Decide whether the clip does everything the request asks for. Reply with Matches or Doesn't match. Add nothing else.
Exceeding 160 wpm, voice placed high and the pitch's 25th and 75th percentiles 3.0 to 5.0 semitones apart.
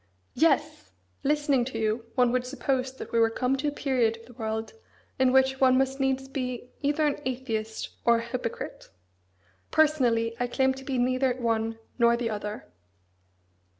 Doesn't match